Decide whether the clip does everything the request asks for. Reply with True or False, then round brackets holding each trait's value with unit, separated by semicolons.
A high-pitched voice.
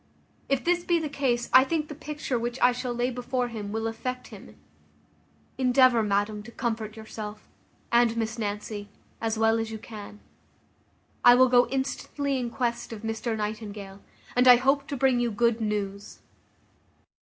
True (235 Hz)